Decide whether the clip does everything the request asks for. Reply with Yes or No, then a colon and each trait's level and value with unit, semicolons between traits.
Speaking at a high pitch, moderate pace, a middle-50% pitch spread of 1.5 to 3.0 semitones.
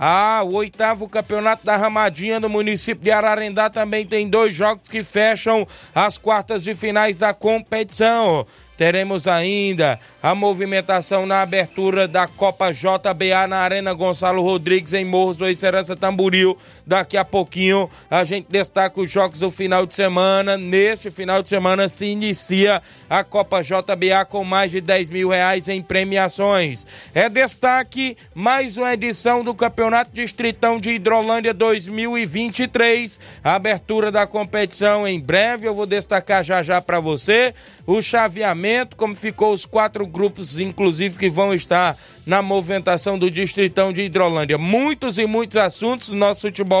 Yes: high, 200 Hz; average, 150 wpm; narrow, 2.5 semitones